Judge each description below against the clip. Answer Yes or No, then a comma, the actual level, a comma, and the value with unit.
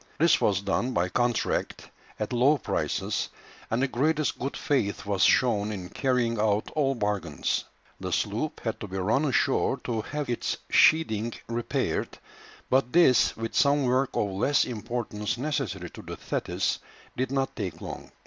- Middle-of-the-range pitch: No, low, 120 Hz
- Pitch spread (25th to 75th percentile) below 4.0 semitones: No, average, 4.7 semitones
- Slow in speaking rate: No, average, 160 wpm